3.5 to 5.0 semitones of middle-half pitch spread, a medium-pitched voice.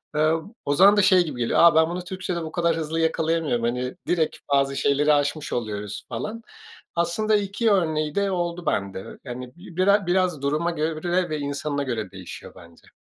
Yes: average, 4.0 semitones; medium, 160 Hz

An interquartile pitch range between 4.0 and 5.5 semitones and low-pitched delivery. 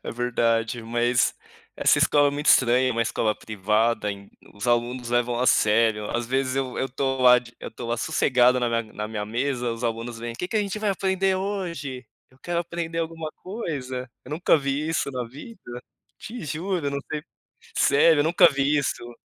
Yes: average, 4.7 semitones; low, 130 Hz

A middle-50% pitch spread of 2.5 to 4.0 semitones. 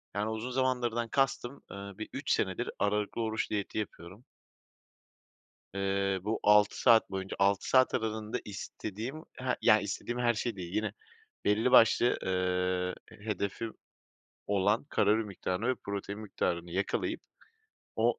Yes: average, 3.0 semitones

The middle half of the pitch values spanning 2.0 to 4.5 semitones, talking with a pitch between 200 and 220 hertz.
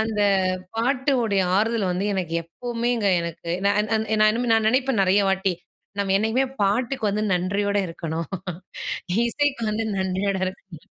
Yes: average, 3.6 semitones; high, 205 Hz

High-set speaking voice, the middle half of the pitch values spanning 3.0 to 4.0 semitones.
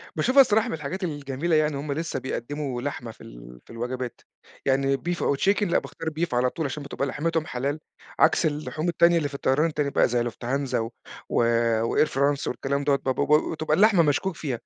No: medium, 145 Hz; average, 3.7 semitones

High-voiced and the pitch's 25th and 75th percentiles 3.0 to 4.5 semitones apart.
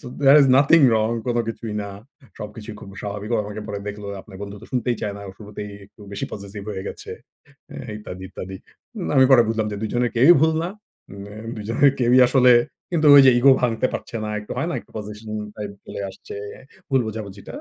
No: low, 110 Hz; average, 3.6 semitones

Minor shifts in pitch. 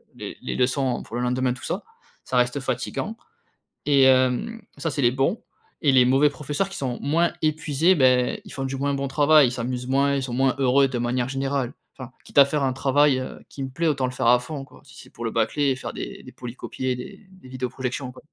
Yes: narrow, 2.2 semitones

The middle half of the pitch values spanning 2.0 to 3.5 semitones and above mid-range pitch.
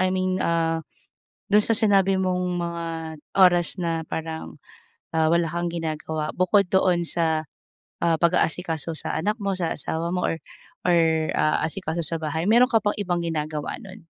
No: narrow, 2.4 semitones; medium, 170 Hz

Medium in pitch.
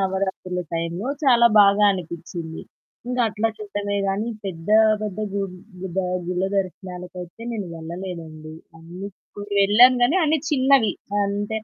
No: high, 195 Hz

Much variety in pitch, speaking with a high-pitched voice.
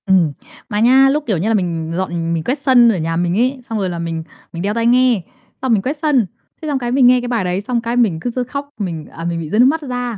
Yes: wide, 6.4 semitones; high, 230 Hz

